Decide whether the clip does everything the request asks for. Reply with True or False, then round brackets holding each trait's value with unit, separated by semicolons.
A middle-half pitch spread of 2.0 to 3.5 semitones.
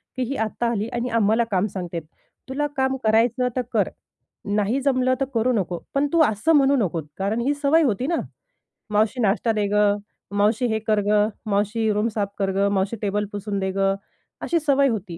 False (4.1 semitones)